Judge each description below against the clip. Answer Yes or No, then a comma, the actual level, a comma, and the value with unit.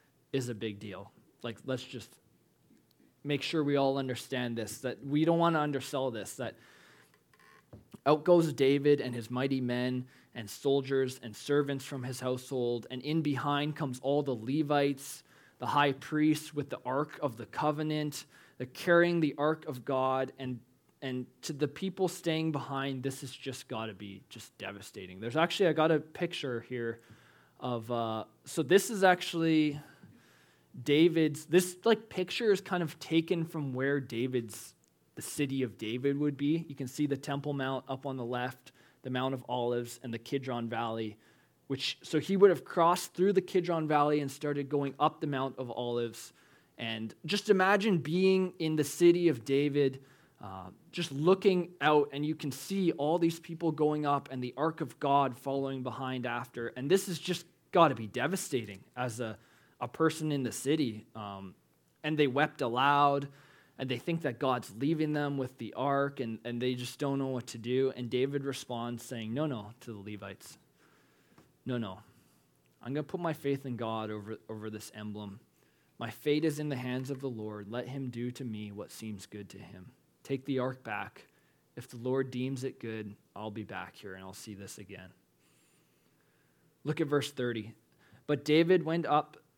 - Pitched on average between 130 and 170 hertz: Yes, low, 135 Hz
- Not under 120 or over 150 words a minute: No, average, 185 wpm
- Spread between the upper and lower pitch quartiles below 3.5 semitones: No, average, 4.0 semitones